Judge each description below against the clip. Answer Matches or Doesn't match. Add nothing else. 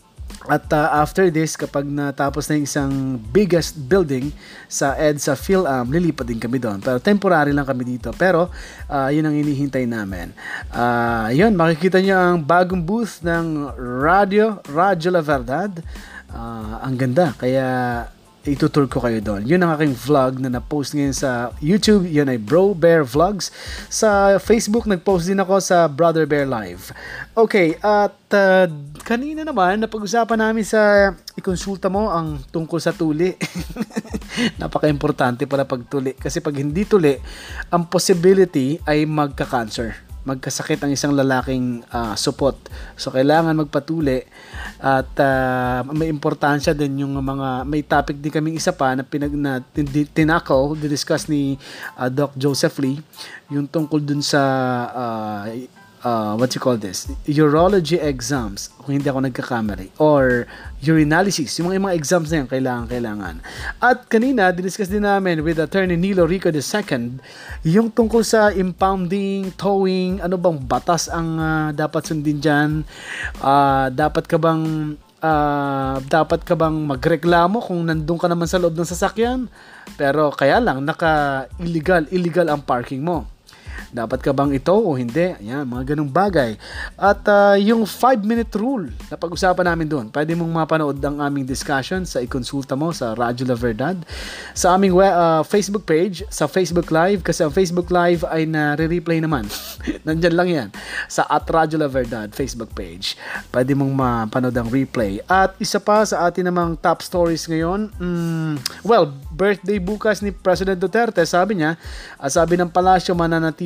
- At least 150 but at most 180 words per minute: Matches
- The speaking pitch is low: Doesn't match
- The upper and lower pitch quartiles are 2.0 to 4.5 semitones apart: Doesn't match